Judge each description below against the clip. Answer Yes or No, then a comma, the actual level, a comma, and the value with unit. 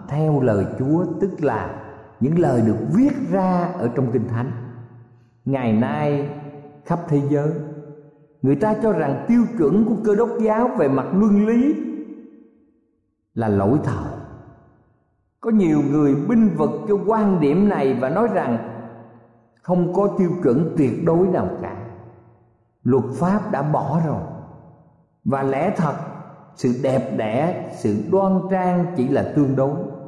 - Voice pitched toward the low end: No, medium, 150 Hz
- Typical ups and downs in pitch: No, wide, 7.1 semitones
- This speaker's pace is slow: Yes, slow, 150 wpm